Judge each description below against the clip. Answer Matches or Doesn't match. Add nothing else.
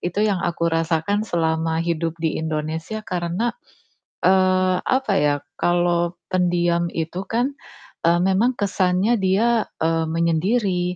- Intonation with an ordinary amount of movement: Matches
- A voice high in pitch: Doesn't match